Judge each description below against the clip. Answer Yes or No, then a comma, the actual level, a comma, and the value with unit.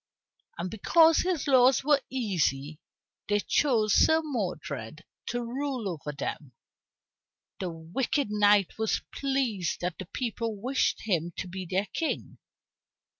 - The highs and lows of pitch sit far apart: Yes, wide, 7.0 semitones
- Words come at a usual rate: No, slow, 125 wpm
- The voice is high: Yes, high, 210 Hz